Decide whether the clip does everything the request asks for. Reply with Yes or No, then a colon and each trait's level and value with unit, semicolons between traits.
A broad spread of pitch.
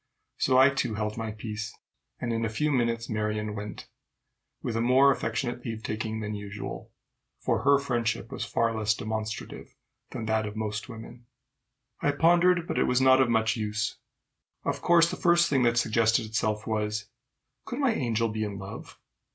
No: average, 3.0 semitones